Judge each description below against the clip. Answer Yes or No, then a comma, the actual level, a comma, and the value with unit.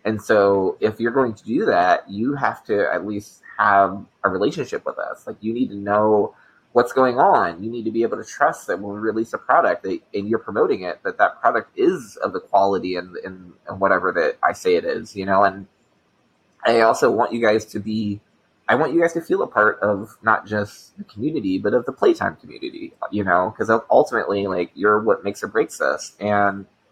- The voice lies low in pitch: Yes, low, 110 Hz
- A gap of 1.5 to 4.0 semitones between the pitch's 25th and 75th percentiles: No, average, 4.6 semitones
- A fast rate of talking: Yes, fast, 220 wpm